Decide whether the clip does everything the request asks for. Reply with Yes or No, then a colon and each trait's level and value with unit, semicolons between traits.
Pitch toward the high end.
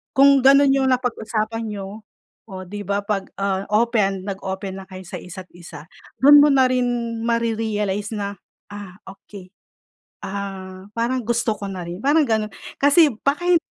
Yes: high, 210 Hz